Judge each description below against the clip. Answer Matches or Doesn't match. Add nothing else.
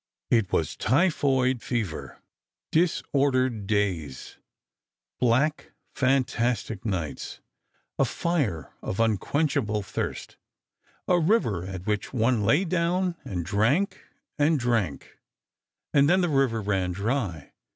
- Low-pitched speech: Matches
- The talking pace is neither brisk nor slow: Doesn't match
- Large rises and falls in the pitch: Matches